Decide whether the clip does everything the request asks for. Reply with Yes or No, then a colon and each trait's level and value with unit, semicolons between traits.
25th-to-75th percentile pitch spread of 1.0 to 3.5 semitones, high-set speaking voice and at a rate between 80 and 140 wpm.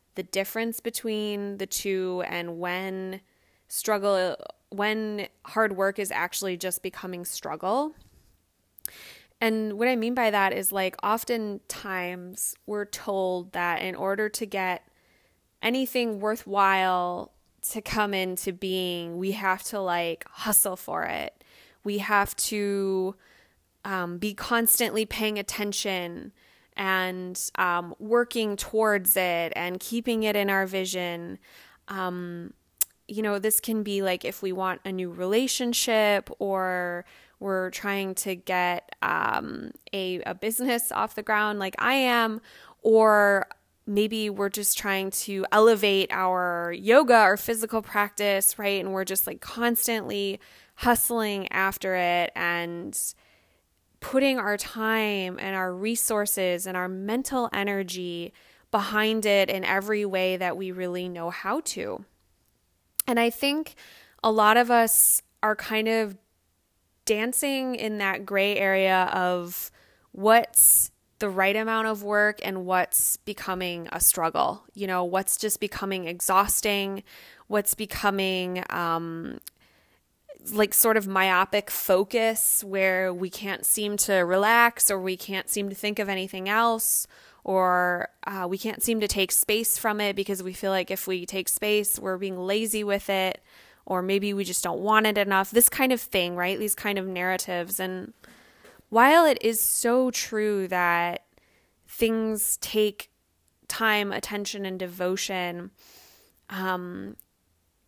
Yes: average, 2.8 semitones; high, 195 Hz; slow, 135 wpm